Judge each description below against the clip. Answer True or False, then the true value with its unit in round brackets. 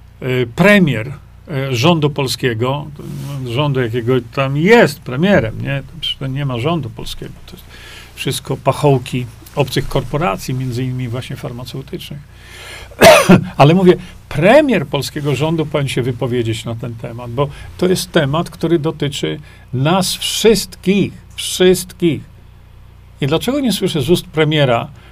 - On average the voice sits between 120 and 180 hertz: True (140 Hz)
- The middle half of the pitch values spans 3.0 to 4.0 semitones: False (4.6 semitones)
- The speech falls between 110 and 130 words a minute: True (120 wpm)